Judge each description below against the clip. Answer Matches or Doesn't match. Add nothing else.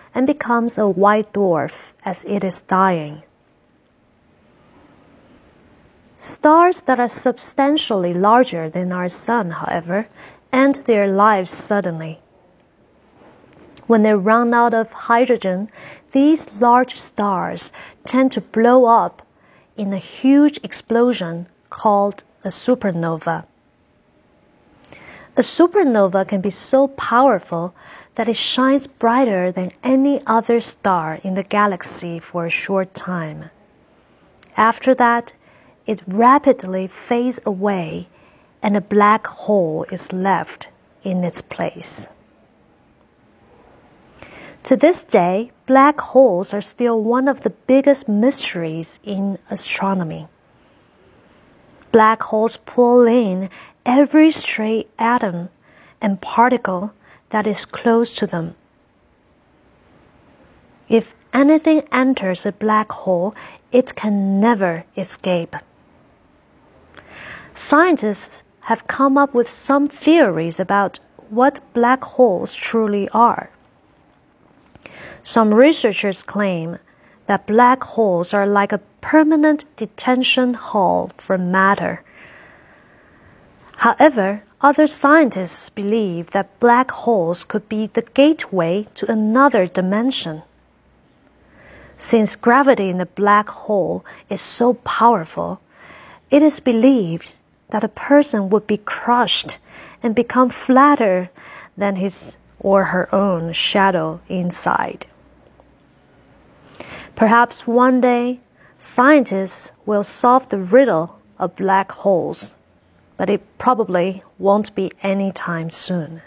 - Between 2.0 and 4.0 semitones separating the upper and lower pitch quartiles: Doesn't match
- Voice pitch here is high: Matches